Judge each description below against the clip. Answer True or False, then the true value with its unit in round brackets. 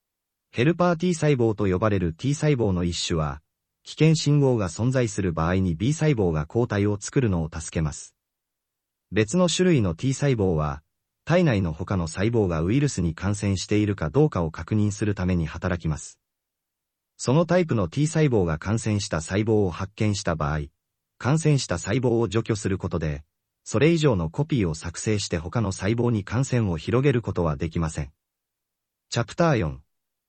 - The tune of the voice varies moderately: False (6.5 semitones)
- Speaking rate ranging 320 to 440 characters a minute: True (325 characters per minute)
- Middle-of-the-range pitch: False (105 Hz)